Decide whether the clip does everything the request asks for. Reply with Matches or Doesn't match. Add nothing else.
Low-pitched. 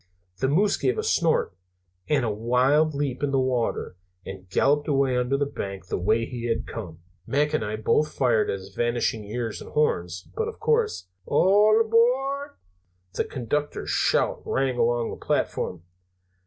Matches